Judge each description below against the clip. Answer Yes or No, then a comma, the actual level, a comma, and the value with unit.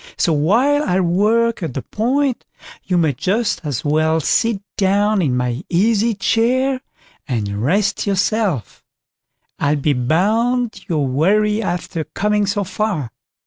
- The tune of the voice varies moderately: No, wide, 6.4 semitones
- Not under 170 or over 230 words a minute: No, slow, 135 wpm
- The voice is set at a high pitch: Yes, high, 195 Hz